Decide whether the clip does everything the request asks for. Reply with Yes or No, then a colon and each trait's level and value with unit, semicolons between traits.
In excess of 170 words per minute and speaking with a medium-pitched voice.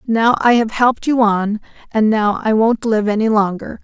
No: fast, 205 wpm; high, 220 Hz